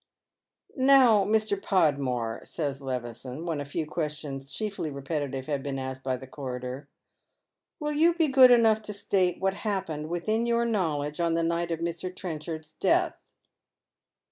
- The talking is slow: No, average, 155 wpm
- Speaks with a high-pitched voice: No, medium, 165 Hz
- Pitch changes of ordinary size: No, wide, 6.7 semitones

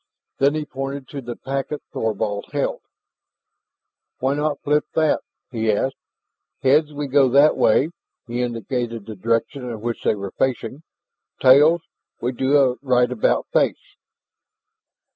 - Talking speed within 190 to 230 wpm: No, average, 140 wpm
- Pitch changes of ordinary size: Yes, average, 3.4 semitones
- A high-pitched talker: No, low, 130 Hz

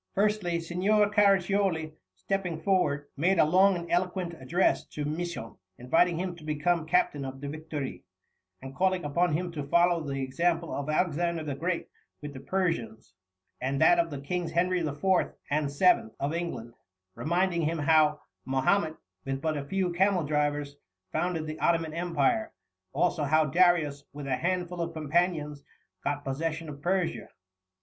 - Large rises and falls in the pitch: No, average, 3.5 semitones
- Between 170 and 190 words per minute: No, average, 155 wpm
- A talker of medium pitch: Yes, medium, 165 Hz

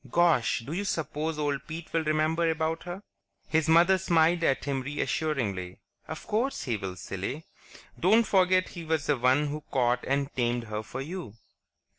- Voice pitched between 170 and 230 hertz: No, medium, 155 Hz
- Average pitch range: Yes, average, 4.7 semitones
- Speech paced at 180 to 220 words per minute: No, average, 170 wpm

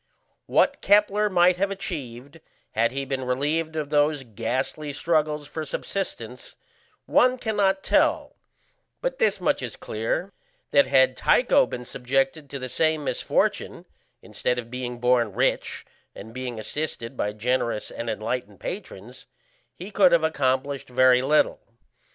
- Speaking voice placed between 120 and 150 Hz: Yes, medium, 140 Hz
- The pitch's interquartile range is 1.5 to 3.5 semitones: No, average, 5.3 semitones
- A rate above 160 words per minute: No, average, 140 wpm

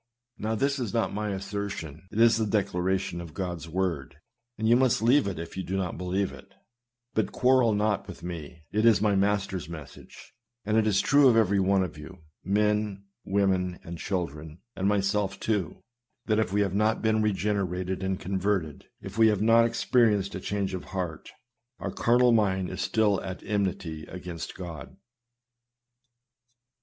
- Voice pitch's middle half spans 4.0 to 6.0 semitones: No, average, 2.8 semitones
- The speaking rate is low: No, average, 175 wpm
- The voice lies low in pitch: Yes, low, 100 Hz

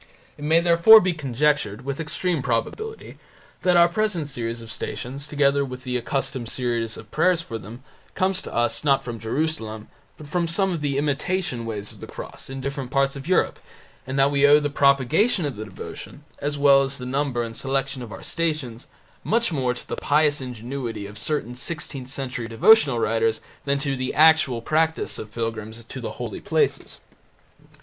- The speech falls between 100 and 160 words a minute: No, average, 185 wpm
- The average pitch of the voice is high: No, medium, 140 Hz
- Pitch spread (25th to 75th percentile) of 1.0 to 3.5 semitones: No, average, 4.5 semitones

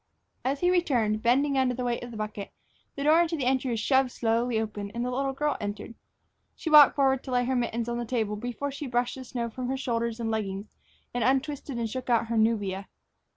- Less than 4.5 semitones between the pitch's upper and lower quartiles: Yes, average, 3.0 semitones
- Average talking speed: No, fast, 230 wpm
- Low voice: No, high, 245 Hz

